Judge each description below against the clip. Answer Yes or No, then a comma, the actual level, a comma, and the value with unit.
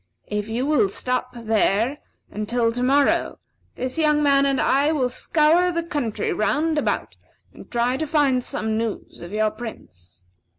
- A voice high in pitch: Yes, very high, 250 Hz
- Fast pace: No, average, 160 wpm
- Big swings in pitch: No, average, 5.0 semitones